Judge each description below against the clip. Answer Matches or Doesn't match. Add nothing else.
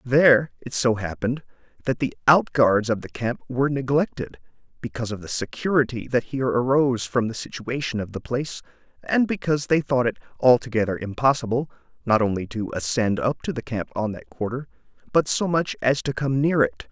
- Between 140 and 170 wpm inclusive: Doesn't match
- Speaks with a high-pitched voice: Doesn't match